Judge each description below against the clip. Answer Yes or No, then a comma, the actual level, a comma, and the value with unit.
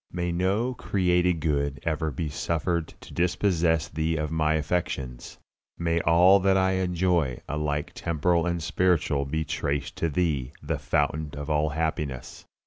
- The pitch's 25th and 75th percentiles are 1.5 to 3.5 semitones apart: Yes, average, 2.9 semitones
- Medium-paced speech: Yes, average, 145 wpm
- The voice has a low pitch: Yes, very low, 80 Hz